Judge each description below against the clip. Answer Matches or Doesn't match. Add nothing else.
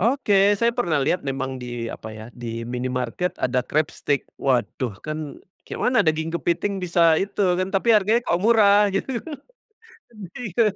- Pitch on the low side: Doesn't match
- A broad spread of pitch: Matches